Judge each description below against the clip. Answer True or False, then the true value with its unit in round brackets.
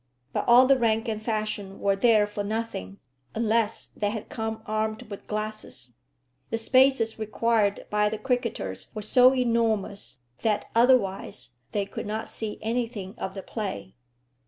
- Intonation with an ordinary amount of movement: False (2.2 semitones)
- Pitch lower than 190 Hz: False (215 Hz)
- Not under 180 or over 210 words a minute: False (150 wpm)